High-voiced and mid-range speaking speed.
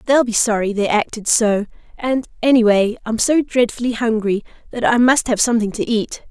Yes: high, 230 Hz; average, 190 wpm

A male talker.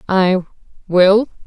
No: female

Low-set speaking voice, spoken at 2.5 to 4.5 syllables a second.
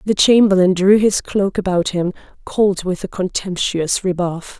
No: high, 190 Hz; 4.3 syllables/s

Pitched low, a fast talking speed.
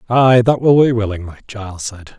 No: low, 110 Hz; average, 190 wpm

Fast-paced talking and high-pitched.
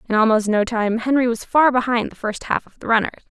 Yes: fast, 250 wpm; high, 230 Hz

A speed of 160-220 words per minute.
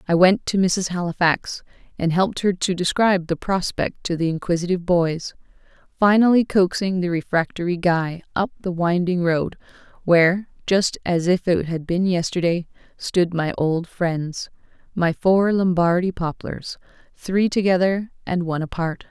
No: average, 145 wpm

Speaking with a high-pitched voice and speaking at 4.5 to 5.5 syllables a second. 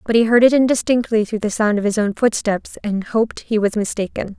No: high, 220 Hz; 5.8 syllables/s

